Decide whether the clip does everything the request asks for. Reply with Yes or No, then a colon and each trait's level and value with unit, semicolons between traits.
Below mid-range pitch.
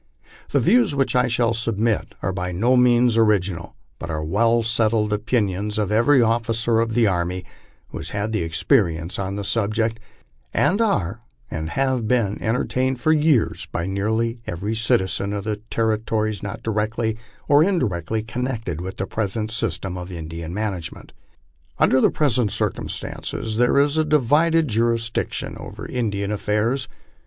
Yes: low, 110 Hz